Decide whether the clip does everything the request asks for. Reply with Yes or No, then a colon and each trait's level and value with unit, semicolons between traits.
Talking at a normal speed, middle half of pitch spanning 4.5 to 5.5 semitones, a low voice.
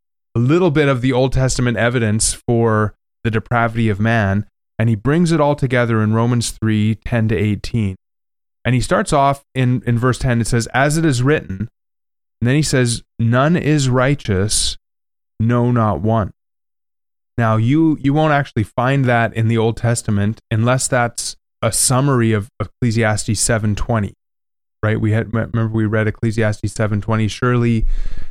No: average, 165 wpm; average, 2.9 semitones; low, 115 Hz